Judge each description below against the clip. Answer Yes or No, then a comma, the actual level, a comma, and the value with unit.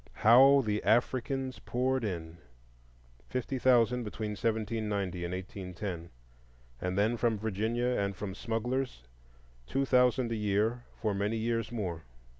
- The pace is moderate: No, slow, 120 wpm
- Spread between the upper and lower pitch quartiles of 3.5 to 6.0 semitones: Yes, average, 4.5 semitones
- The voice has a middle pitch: No, low, 110 Hz